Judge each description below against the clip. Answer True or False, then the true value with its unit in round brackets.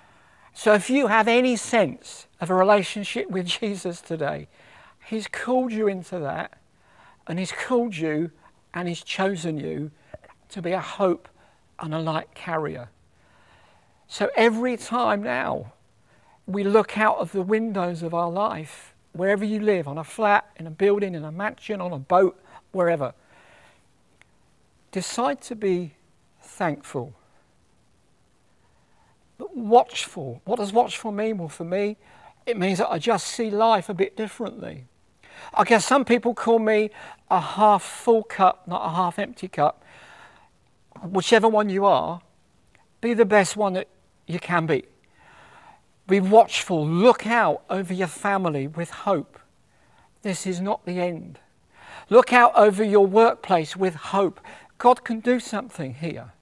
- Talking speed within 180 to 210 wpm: False (145 wpm)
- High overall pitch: True (195 Hz)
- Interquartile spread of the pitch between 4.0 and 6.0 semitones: True (4.4 semitones)